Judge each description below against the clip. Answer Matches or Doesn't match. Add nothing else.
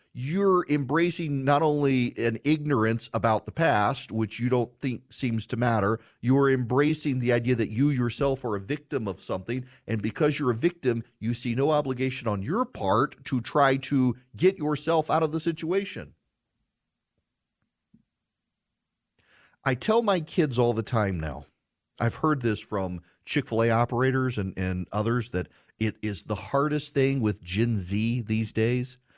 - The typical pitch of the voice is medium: Doesn't match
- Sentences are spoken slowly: Doesn't match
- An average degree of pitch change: Matches